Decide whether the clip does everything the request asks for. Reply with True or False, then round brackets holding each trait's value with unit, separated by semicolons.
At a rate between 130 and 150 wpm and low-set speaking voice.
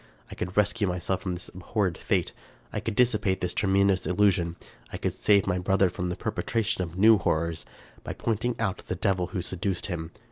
False (190 wpm; 95 Hz)